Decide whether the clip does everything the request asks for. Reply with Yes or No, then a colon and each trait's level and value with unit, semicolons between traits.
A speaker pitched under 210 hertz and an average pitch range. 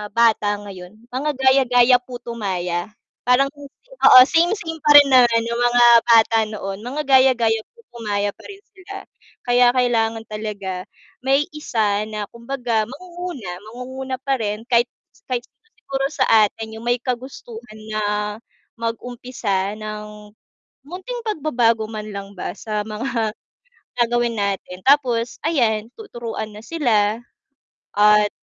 No: high, 235 Hz; average, 3.9 semitones